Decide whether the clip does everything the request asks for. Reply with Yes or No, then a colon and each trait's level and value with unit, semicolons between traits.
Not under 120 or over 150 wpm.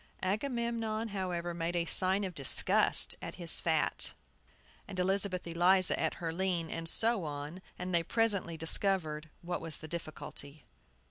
Yes: average, 145 wpm